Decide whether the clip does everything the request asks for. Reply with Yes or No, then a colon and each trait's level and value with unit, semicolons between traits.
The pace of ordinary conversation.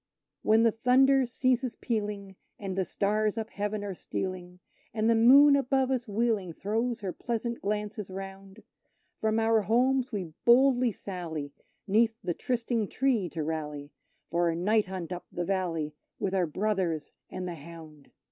Yes: average, 155 wpm